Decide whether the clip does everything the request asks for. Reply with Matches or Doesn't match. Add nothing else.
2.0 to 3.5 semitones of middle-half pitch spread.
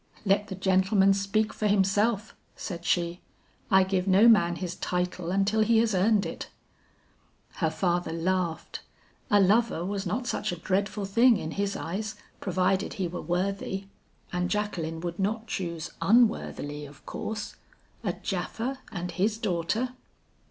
Matches